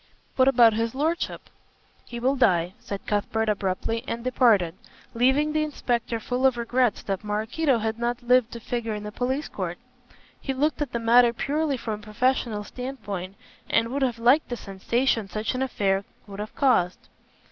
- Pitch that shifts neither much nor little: Yes, average, 3.6 semitones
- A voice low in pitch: No, high, 235 Hz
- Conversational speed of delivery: Yes, average, 175 wpm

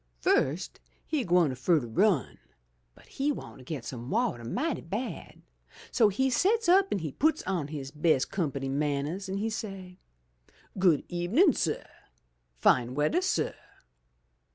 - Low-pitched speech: No, medium, 175 Hz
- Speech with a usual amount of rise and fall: No, wide, 8.6 semitones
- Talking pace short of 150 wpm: No, average, 155 wpm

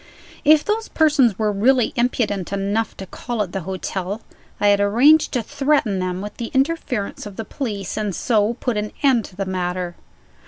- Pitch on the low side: No, high, 210 Hz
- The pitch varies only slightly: No, average, 4.3 semitones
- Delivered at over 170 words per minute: Yes, average, 190 wpm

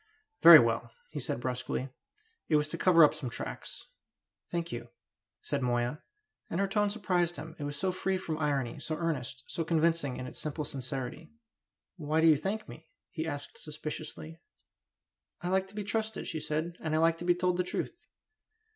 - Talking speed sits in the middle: Yes, average, 185 wpm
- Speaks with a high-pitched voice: No, medium, 160 Hz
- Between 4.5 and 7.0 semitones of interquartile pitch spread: No, average, 3.5 semitones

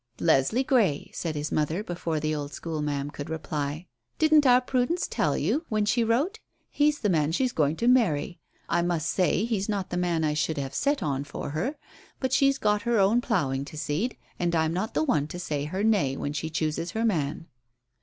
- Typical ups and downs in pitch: No, wide, 7.3 semitones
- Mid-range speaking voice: Yes, medium, 175 Hz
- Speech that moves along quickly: Yes, fast, 210 wpm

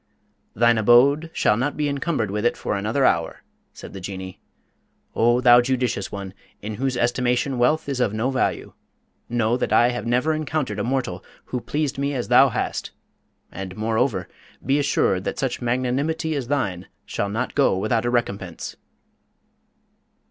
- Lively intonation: No, average, 4.3 semitones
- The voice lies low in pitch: Yes, low, 120 Hz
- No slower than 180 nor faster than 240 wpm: No, average, 165 wpm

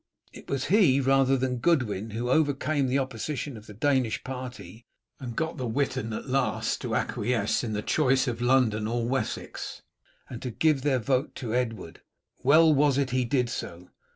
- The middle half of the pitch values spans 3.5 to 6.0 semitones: No, average, 2.9 semitones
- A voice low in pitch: Yes, low, 130 Hz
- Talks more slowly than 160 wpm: No, average, 180 wpm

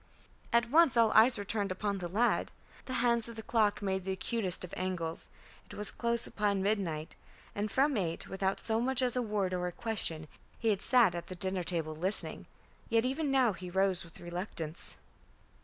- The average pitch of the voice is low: No, high, 205 Hz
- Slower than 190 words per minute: No, average, 195 wpm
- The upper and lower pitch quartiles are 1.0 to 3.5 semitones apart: No, average, 4.3 semitones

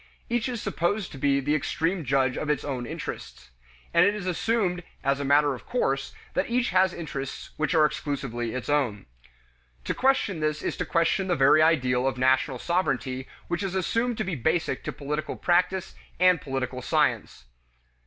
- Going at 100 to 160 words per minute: No, average, 175 wpm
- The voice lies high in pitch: No, medium, 155 Hz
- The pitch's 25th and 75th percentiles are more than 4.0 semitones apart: Yes, wide, 5.4 semitones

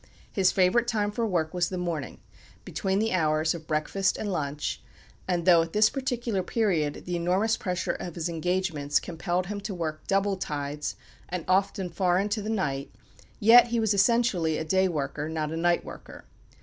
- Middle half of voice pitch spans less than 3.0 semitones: No, average, 4.1 semitones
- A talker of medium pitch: Yes, medium, 180 Hz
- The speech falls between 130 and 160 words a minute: No, average, 180 wpm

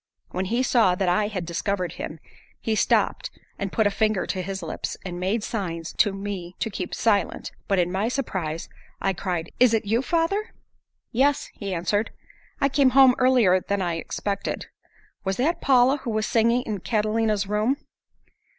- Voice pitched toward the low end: No, high, 205 Hz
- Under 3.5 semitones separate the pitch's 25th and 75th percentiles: No, average, 4.3 semitones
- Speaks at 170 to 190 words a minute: Yes, average, 175 wpm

